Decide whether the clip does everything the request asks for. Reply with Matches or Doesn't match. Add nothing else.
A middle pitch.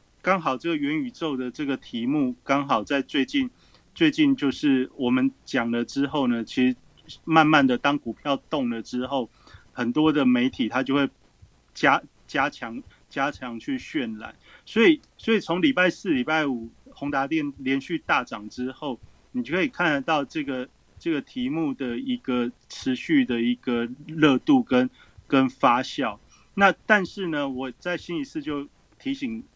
Matches